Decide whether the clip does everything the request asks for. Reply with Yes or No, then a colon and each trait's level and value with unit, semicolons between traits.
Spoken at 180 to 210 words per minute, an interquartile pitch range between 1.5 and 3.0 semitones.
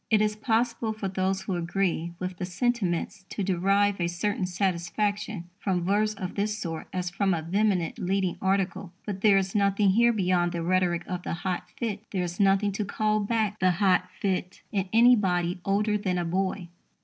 Yes: average, 185 wpm; narrow, 2.6 semitones